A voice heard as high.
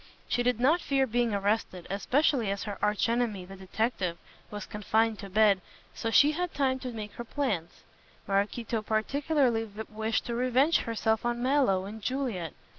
Yes: high, 225 Hz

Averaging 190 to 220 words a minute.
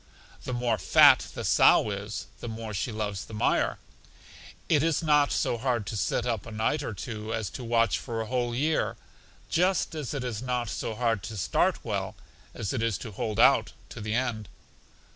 Yes: average, 200 wpm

